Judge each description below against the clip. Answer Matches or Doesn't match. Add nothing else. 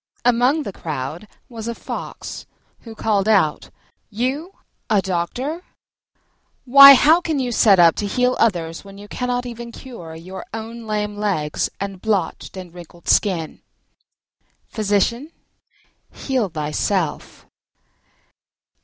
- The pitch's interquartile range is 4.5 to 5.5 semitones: Matches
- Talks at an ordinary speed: Doesn't match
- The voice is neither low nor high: Doesn't match